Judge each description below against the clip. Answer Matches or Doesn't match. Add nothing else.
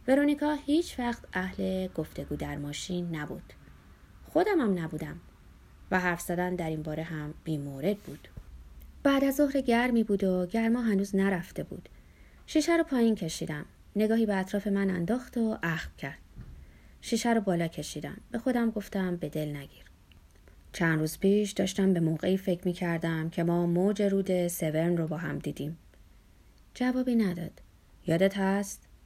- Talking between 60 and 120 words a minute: Doesn't match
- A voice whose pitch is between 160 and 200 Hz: Matches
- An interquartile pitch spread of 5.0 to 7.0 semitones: Matches